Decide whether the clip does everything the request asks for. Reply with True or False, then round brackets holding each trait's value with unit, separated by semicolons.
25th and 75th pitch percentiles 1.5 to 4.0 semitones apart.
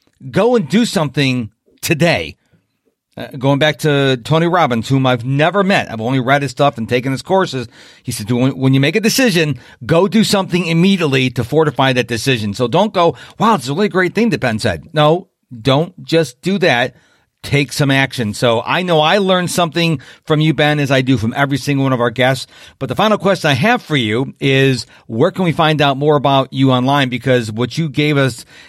False (4.7 semitones)